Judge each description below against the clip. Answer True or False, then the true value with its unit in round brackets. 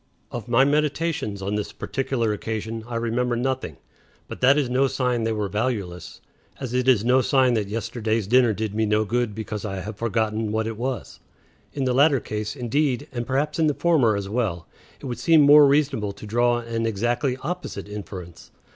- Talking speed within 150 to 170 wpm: False (190 wpm)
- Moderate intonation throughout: True (3.6 semitones)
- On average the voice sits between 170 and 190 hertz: False (115 Hz)